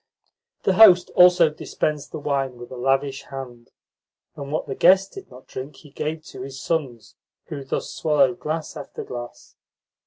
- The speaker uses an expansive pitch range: No, average, 3.5 semitones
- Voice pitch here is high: No, medium, 145 Hz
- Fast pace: No, average, 165 wpm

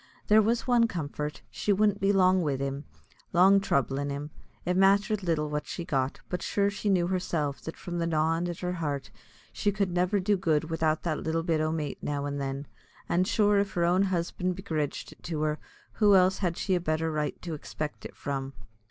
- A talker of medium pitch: Yes, medium, 170 Hz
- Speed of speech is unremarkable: No, fast, 210 wpm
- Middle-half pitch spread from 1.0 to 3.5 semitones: No, average, 4.1 semitones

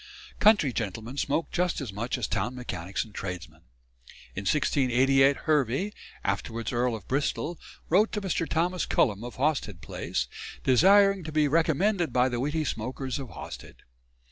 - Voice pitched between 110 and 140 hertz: Yes, low, 135 Hz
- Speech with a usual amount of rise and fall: No, wide, 5.9 semitones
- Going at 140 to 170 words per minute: Yes, average, 150 wpm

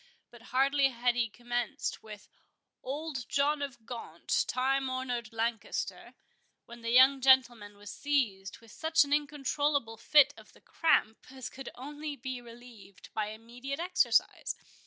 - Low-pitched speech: No, very high, 255 Hz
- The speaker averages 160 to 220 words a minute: No, average, 140 wpm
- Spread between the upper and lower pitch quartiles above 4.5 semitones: No, average, 3.4 semitones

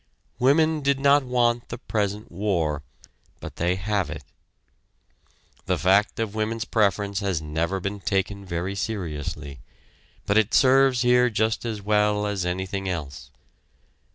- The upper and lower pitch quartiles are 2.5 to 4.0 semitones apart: Yes, average, 3.6 semitones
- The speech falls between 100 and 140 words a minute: Yes, slow, 135 wpm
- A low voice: Yes, low, 105 Hz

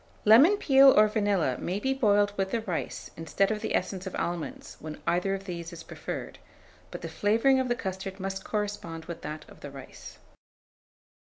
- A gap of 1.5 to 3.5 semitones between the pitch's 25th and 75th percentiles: No, average, 3.9 semitones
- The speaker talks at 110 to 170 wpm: No, average, 185 wpm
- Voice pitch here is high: Yes, high, 195 Hz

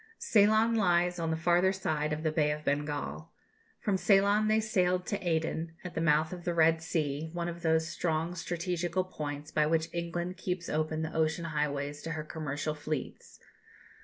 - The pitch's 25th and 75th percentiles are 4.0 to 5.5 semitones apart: No, narrow, 2.6 semitones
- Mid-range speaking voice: Yes, medium, 165 Hz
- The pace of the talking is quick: No, average, 180 wpm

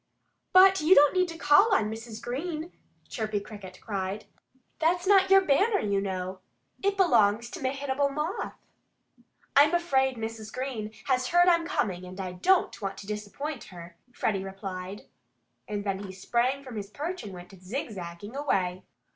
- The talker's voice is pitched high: Yes, high, 235 Hz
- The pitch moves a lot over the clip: Yes, wide, 7.8 semitones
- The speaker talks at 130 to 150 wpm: No, average, 160 wpm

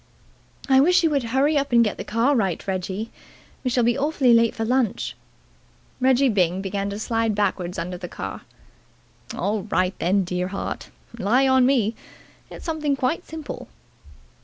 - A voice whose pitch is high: Yes, high, 230 Hz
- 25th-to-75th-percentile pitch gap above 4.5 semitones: Yes, average, 5.3 semitones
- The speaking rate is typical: Yes, average, 160 wpm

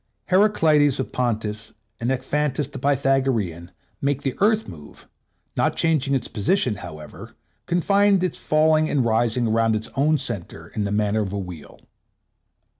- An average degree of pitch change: No, wide, 6.3 semitones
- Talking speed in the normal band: Yes, average, 150 wpm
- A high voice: No, low, 130 Hz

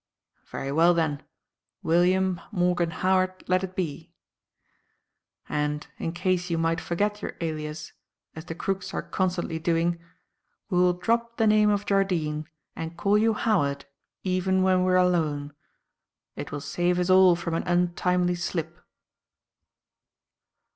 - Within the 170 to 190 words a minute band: No, average, 140 wpm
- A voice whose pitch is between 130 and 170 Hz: No, medium, 180 Hz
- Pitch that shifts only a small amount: Yes, narrow, 2.3 semitones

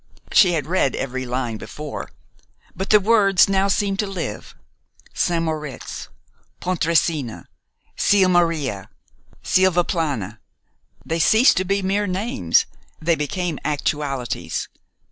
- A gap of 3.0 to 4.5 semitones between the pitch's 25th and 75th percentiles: No, average, 5.2 semitones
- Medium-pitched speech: Yes, medium, 170 Hz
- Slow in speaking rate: Yes, slow, 110 wpm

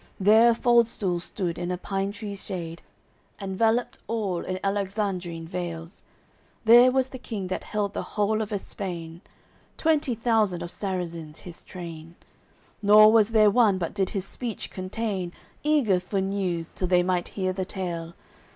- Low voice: No, high, 195 Hz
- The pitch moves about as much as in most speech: Yes, average, 3.5 semitones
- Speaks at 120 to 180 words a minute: Yes, average, 160 wpm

